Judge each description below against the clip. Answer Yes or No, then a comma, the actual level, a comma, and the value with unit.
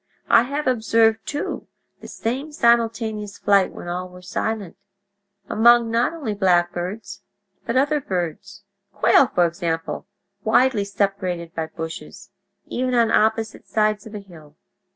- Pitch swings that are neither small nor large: Yes, average, 4.3 semitones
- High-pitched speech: Yes, high, 215 Hz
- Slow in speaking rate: Yes, slow, 125 wpm